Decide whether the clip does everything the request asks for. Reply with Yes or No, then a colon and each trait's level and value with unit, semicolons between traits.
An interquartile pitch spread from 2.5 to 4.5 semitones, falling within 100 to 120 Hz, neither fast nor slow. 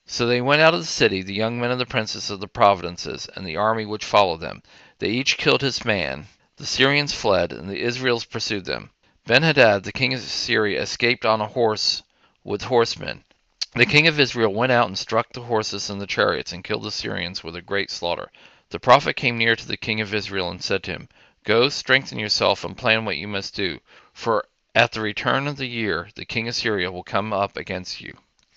No: average, 3.2 semitones; low, 110 Hz; fast, 220 wpm